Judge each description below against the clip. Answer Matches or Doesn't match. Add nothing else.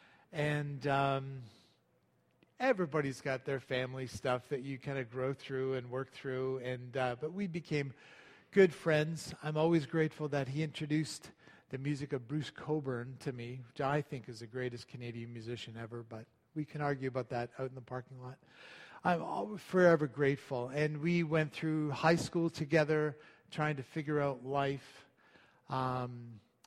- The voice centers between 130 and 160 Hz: Matches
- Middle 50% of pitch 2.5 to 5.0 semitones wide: Matches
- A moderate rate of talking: Matches